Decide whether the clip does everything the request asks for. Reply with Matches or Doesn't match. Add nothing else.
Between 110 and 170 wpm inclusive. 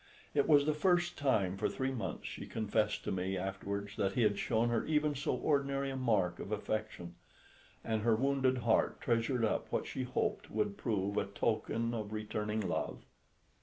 Doesn't match